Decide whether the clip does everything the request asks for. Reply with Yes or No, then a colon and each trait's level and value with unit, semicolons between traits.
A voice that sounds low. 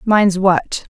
No: high, 190 Hz